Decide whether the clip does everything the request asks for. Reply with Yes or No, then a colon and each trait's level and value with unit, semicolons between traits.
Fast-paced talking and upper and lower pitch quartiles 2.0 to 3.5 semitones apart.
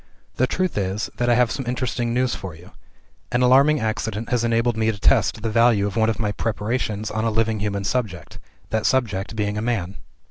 Yes: fast, 210 wpm; average, 2.8 semitones